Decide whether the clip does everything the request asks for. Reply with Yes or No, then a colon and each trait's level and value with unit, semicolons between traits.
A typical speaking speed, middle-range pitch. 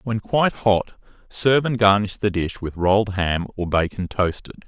No: average, 180 wpm; low, 100 Hz